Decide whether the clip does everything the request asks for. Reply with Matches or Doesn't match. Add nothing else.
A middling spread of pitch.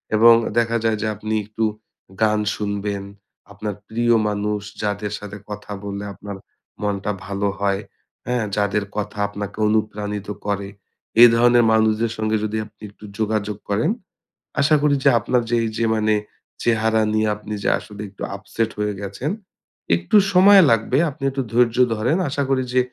Doesn't match